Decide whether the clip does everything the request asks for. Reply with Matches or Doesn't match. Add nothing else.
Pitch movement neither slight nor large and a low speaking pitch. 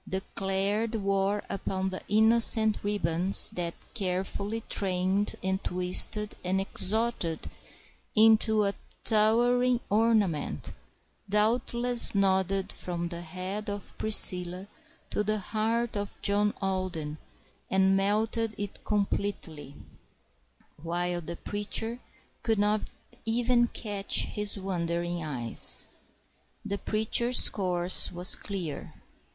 Doesn't match